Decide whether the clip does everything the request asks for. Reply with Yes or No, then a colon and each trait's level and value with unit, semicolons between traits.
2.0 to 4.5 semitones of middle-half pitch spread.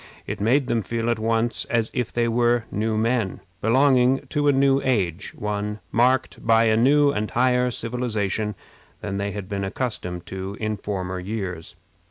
Yes: average, 3.4 semitones